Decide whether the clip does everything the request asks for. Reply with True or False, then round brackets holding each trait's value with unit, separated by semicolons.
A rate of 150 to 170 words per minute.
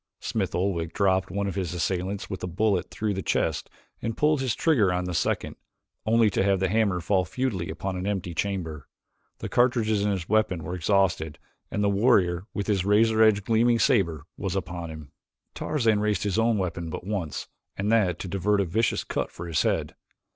False (195 wpm)